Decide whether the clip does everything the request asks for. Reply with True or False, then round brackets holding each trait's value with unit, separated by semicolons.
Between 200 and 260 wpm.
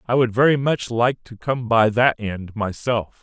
True (205 wpm)